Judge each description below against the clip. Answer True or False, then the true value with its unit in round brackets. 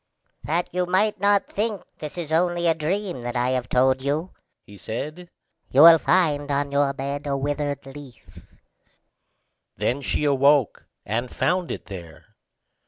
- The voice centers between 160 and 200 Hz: False (145 Hz)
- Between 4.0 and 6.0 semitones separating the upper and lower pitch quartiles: True (4.6 semitones)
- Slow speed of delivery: False (155 wpm)